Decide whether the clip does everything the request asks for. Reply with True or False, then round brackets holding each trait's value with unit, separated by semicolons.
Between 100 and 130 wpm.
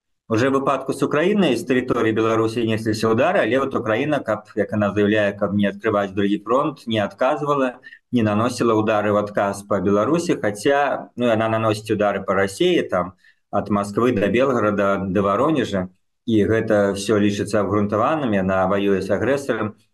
False (155 wpm)